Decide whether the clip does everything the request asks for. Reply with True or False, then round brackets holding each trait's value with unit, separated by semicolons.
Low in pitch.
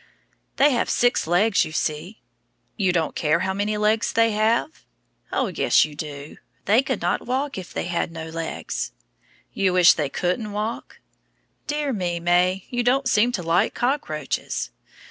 False (195 Hz)